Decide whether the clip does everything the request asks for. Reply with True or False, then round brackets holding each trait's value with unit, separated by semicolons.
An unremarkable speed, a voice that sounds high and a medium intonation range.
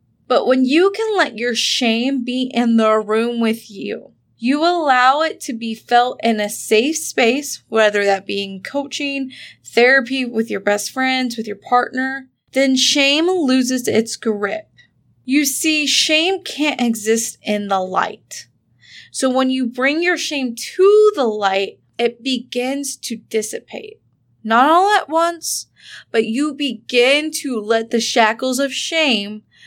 True (150 wpm; 255 Hz; 4.1 semitones)